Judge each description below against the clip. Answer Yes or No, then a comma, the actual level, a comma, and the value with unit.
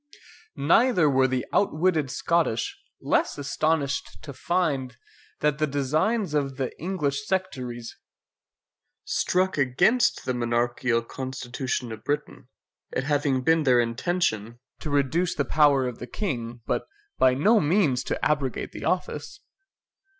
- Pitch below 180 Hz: Yes, medium, 140 Hz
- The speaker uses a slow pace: Yes, slow, 130 wpm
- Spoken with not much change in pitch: No, average, 4.2 semitones